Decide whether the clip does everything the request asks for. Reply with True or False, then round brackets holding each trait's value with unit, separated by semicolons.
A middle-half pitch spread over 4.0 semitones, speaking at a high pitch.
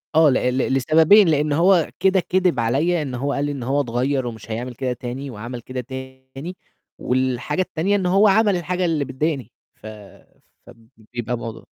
False (5.3 semitones; 135 Hz)